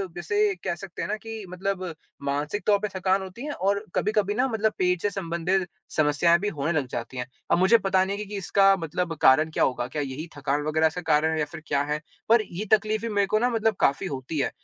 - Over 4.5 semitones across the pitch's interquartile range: Yes, average, 4.9 semitones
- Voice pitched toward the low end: No, medium, 185 Hz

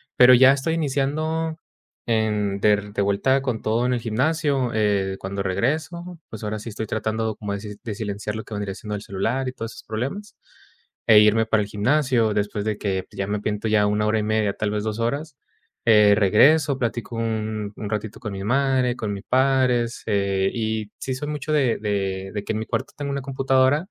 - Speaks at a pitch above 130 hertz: No, low, 110 Hz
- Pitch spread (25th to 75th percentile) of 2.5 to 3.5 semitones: No, average, 4.1 semitones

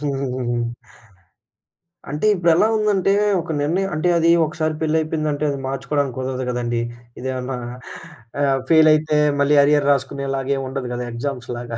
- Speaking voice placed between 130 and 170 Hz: Yes, medium, 140 Hz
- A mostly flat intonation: No, average, 3.2 semitones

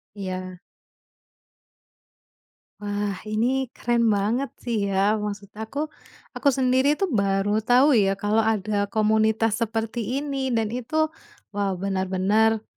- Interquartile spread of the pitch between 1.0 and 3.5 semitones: Yes, average, 3.2 semitones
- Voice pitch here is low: No, high, 215 Hz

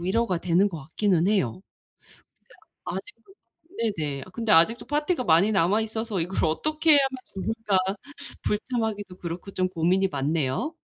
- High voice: Yes, high, 195 Hz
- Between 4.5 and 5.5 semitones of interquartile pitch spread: Yes, average, 5.2 semitones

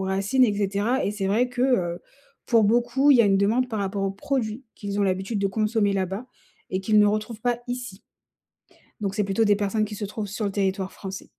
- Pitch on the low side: No, high, 210 Hz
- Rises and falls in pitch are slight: No, average, 3.0 semitones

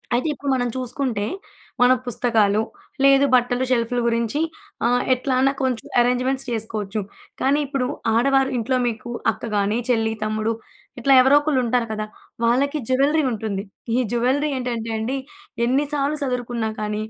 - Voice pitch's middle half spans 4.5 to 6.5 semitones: No, average, 3.0 semitones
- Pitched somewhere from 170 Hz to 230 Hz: No, high, 245 Hz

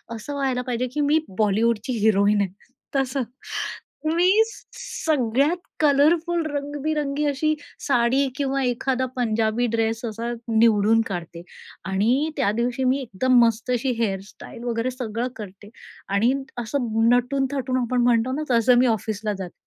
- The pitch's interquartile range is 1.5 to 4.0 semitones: Yes, average, 3.7 semitones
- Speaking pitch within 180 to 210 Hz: No, high, 245 Hz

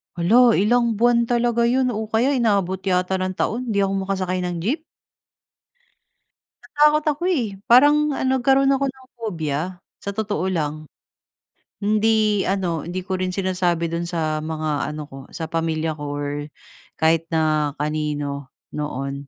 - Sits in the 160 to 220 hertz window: Yes, medium, 185 Hz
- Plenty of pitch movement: Yes, wide, 6.6 semitones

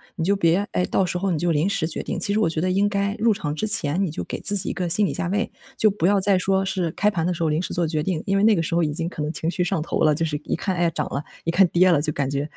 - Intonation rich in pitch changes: No, average, 3.5 semitones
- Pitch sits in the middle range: Yes, medium, 175 Hz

